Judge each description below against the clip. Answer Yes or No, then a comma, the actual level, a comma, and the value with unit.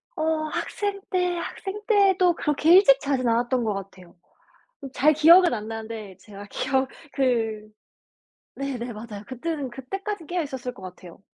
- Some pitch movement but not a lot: No, wide, 7.2 semitones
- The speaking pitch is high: Yes, very high, 265 Hz